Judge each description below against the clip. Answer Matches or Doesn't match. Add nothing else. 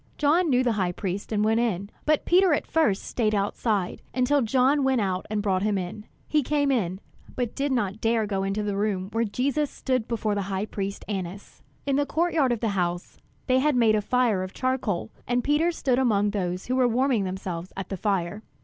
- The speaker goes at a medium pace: Doesn't match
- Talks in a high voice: Matches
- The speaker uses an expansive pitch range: Doesn't match